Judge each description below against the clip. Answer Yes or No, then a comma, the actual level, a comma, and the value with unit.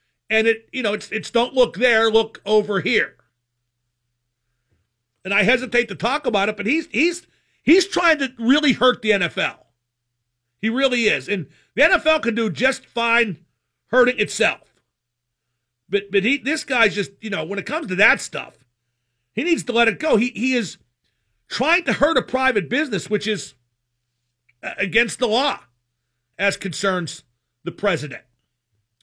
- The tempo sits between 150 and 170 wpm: Yes, average, 165 wpm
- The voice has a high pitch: Yes, high, 205 Hz